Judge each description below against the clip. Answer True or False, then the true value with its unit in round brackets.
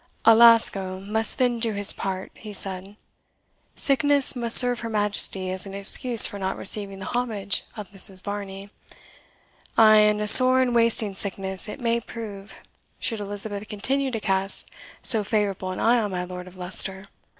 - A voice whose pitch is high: True (205 Hz)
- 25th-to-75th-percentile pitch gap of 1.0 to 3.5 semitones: True (3.0 semitones)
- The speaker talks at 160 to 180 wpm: True (165 wpm)